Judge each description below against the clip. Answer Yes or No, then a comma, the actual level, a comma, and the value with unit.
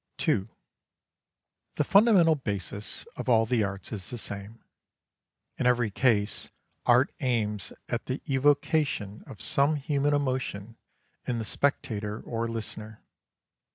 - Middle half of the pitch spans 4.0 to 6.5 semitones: Yes, average, 5.0 semitones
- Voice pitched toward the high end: No, low, 115 Hz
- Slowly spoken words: Yes, slow, 120 wpm